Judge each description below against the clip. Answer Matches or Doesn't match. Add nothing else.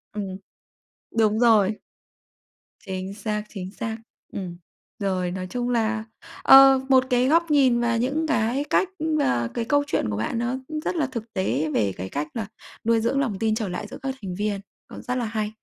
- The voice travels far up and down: Doesn't match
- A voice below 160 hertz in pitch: Doesn't match